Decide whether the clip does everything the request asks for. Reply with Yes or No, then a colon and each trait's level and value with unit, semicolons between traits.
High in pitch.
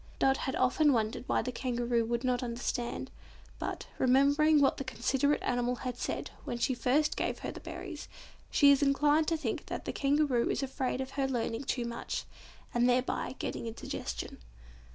Yes: very high, 255 Hz